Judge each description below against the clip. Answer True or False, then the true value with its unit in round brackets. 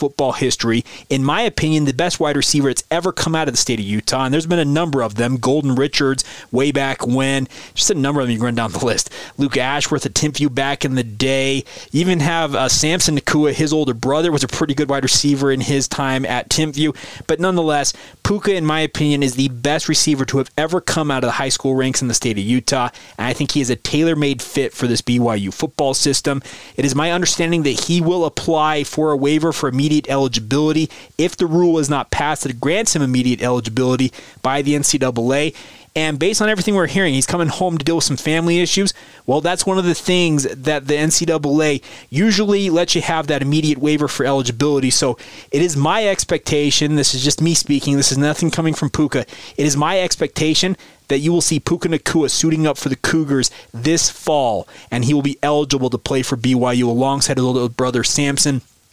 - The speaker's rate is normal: False (220 wpm)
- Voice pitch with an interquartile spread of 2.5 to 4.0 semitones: True (3.0 semitones)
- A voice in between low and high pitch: True (145 Hz)